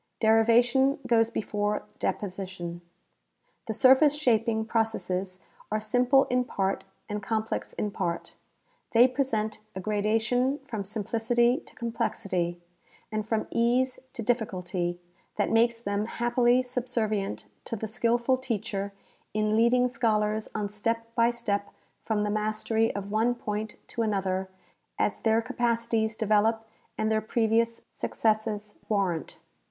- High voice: Yes, high, 220 Hz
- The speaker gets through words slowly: Yes, slow, 125 wpm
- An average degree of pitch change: No, narrow, 2.2 semitones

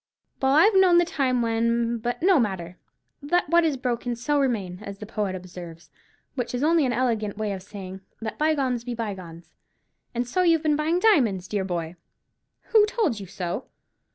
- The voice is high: Yes, high, 235 Hz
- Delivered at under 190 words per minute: Yes, average, 180 wpm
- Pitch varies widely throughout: Yes, wide, 7.3 semitones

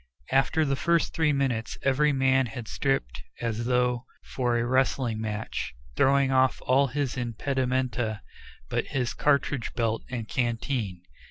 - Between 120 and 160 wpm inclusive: Yes, average, 140 wpm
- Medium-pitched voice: No, low, 125 Hz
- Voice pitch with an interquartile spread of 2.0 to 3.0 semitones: Yes, average, 2.7 semitones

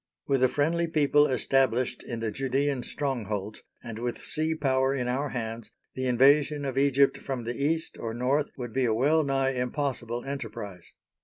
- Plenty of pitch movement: No, average, 2.9 semitones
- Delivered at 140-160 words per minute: No, average, 170 wpm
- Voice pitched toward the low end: Yes, low, 130 Hz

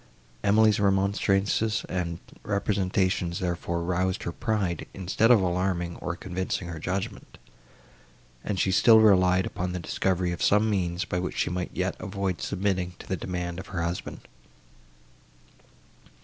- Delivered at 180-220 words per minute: No, average, 140 wpm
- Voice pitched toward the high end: No, very low, 95 Hz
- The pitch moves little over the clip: Yes, narrow, 2.0 semitones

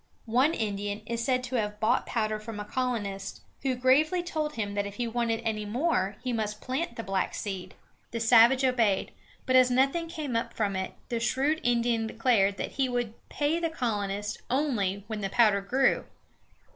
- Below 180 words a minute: No, average, 185 wpm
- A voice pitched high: Yes, high, 230 Hz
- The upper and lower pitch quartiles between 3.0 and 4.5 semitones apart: Yes, average, 3.8 semitones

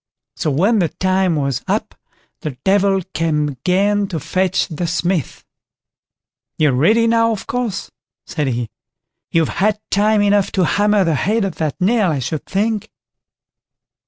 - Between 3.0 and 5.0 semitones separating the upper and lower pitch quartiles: Yes, average, 4.7 semitones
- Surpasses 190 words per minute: No, average, 150 wpm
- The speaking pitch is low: No, medium, 185 Hz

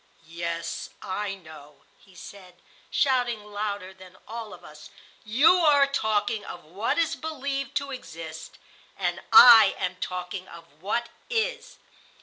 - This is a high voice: Yes, high, 205 Hz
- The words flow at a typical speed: No, slow, 130 wpm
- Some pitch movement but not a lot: No, wide, 6.5 semitones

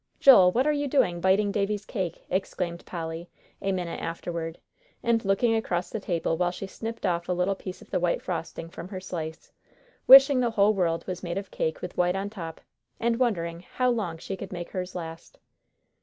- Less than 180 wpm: No, average, 200 wpm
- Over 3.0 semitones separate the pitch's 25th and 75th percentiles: Yes, average, 3.6 semitones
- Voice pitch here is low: No, medium, 185 Hz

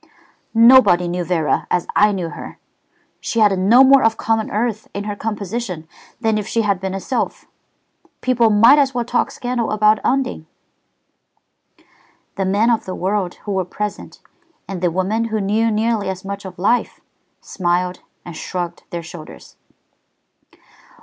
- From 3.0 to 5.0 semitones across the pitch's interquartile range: Yes, average, 3.7 semitones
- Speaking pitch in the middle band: No, high, 205 Hz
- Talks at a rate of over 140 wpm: Yes, average, 155 wpm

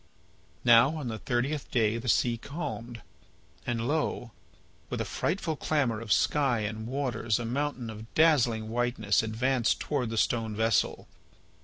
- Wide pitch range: No, average, 3.5 semitones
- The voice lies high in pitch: No, low, 120 Hz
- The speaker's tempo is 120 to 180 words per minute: Yes, average, 145 wpm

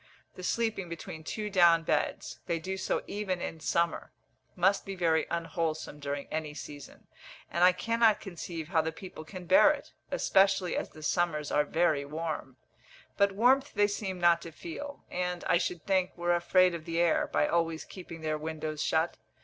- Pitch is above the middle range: No, medium, 170 Hz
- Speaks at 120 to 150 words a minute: No, average, 180 wpm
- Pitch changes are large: No, average, 3.0 semitones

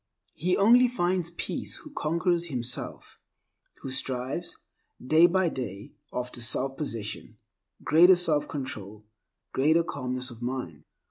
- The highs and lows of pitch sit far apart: Yes, wide, 5.7 semitones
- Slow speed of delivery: Yes, slow, 115 wpm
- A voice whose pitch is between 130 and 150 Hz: Yes, medium, 140 Hz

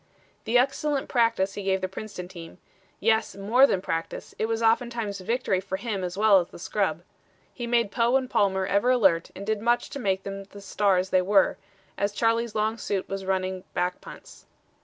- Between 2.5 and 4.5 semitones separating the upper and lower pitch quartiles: Yes, average, 3.4 semitones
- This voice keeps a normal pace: Yes, average, 195 wpm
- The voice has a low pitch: No, high, 200 Hz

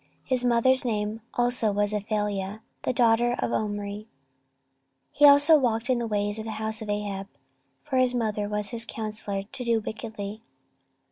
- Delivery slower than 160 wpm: No, average, 165 wpm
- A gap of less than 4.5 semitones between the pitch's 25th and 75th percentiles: Yes, average, 2.7 semitones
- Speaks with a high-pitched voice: Yes, high, 220 Hz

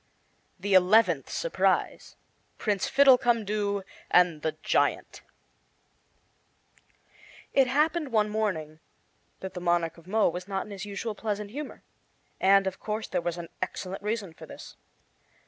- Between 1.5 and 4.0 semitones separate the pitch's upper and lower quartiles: Yes, average, 3.5 semitones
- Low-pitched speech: No, high, 200 Hz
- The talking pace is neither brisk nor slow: No, slow, 130 wpm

